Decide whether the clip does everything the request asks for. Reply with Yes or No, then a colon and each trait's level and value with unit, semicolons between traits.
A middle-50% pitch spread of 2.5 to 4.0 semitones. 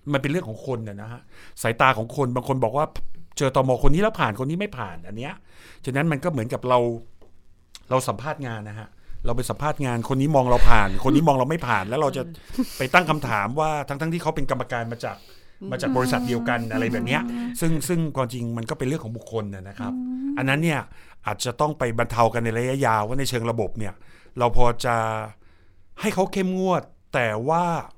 No: average, 4.7 semitones